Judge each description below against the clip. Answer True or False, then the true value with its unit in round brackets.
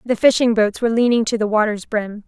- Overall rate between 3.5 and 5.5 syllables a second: False (6.0 syllables/s)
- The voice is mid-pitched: False (220 Hz)